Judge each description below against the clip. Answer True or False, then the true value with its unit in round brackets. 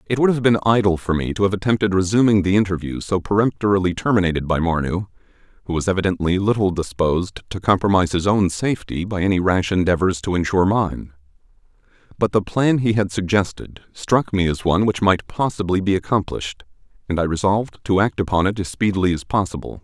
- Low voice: True (95 Hz)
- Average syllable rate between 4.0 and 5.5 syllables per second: False (6.2 syllables/s)